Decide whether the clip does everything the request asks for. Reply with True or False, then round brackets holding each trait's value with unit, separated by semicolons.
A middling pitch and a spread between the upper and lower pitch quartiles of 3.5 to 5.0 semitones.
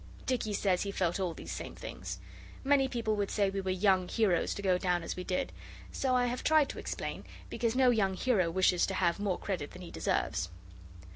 False (195 Hz; 4.6 semitones)